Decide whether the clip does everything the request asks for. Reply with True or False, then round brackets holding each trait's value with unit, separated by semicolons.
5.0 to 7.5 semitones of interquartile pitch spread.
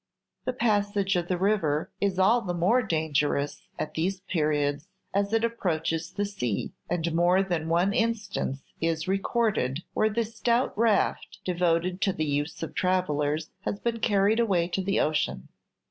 False (4.3 semitones)